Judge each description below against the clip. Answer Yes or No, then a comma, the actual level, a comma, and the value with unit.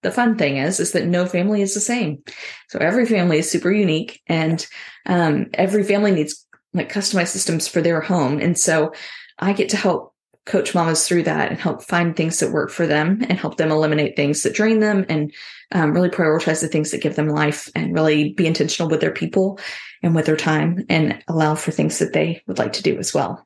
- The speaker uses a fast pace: Yes, fast, 225 wpm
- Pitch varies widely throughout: No, average, 3.6 semitones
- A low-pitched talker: No, medium, 170 Hz